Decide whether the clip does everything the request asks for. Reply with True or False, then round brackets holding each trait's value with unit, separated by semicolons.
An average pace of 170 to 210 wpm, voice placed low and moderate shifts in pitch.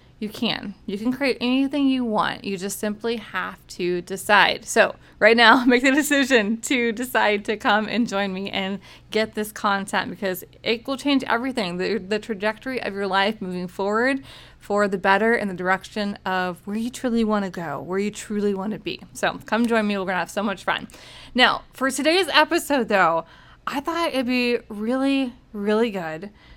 False (195 wpm; 215 Hz; 3.7 semitones)